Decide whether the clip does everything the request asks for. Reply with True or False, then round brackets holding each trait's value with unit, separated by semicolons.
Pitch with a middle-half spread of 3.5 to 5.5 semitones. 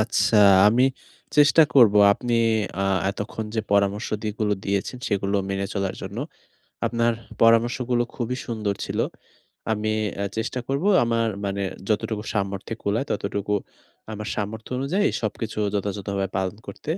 False (2.7 semitones)